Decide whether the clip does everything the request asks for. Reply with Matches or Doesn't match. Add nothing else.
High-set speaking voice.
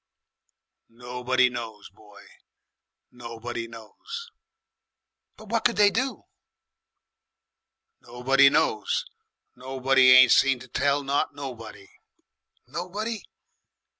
Doesn't match